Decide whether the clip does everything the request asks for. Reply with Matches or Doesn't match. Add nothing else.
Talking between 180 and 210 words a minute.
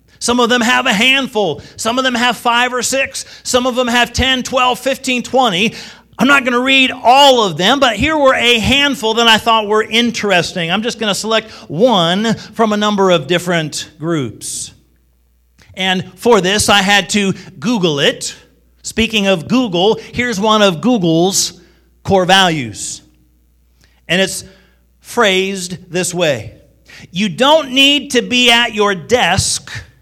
Doesn't match